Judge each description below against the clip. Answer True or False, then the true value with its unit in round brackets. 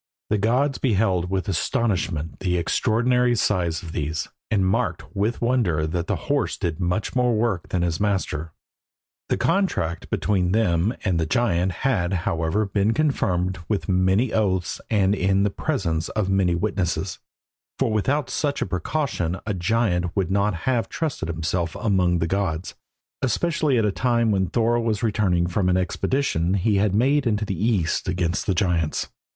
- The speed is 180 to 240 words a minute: False (165 wpm)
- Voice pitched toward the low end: True (95 Hz)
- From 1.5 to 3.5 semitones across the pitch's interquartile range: False (4.5 semitones)